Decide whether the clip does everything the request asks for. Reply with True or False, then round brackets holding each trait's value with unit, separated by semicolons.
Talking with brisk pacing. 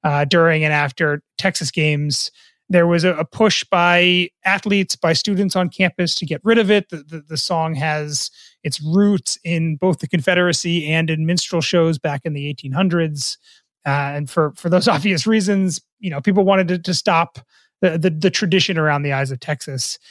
False (190 wpm)